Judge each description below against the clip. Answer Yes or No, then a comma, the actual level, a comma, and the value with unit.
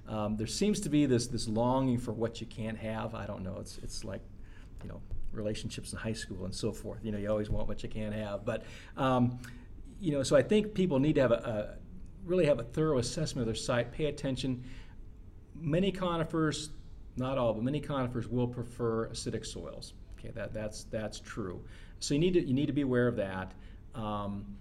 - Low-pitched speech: Yes, low, 115 Hz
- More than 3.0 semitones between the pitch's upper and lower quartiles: Yes, average, 4.1 semitones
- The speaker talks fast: Yes, fast, 215 wpm